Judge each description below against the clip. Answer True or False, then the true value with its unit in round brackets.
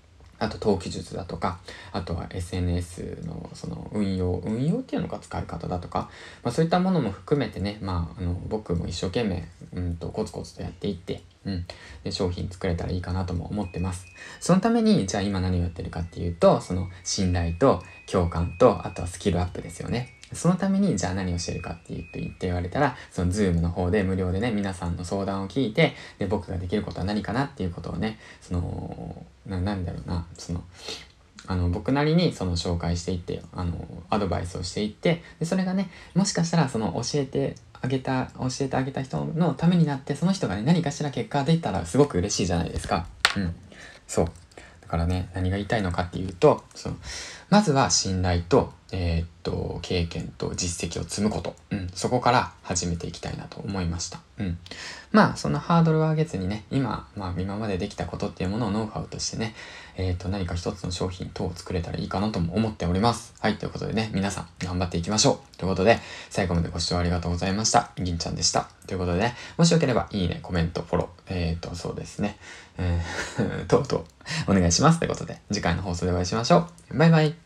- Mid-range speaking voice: False (95 Hz)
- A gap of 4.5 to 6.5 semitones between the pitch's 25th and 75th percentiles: True (5.2 semitones)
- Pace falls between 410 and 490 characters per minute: True (430 characters per minute)